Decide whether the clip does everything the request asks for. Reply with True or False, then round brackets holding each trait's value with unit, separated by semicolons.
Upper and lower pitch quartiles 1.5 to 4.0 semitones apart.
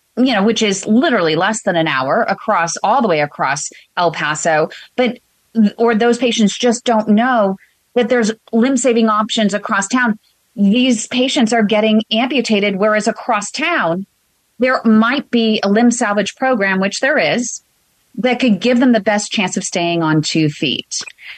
True (3.6 semitones)